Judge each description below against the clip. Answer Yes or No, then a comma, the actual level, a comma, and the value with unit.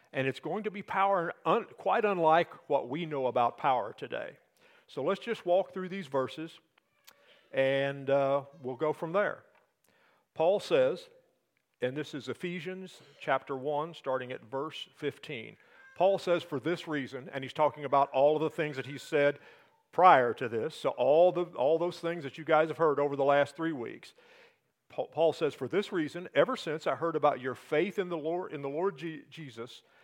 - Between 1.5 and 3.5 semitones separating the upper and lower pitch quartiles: No, average, 5.0 semitones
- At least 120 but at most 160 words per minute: No, average, 190 wpm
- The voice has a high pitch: No, medium, 160 Hz